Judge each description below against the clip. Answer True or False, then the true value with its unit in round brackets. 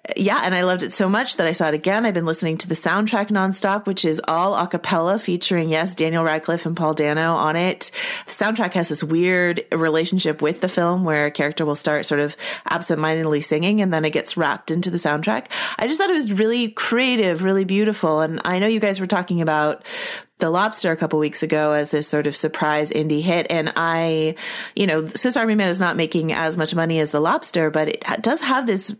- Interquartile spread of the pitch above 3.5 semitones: True (4.0 semitones)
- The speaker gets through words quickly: True (230 wpm)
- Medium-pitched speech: True (170 Hz)